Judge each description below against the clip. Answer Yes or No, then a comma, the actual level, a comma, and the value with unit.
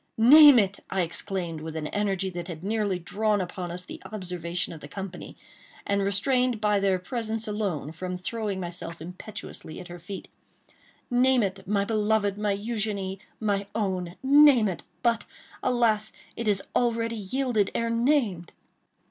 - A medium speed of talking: Yes, average, 150 wpm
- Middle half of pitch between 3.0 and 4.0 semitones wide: Yes, average, 3.7 semitones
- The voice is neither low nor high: No, high, 200 Hz